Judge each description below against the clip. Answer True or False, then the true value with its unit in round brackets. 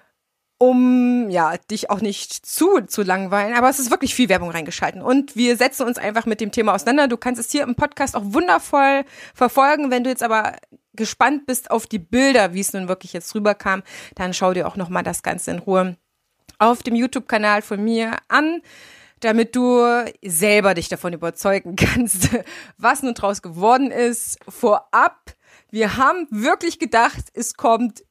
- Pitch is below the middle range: False (230 Hz)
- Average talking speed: True (180 wpm)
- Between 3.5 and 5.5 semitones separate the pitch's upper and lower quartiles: True (4.1 semitones)